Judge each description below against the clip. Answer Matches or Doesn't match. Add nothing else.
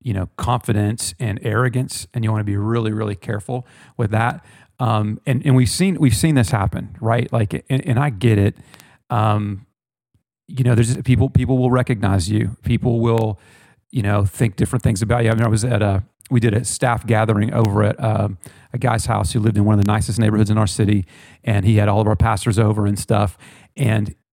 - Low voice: Matches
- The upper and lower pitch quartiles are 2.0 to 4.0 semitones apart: Matches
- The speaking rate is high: Matches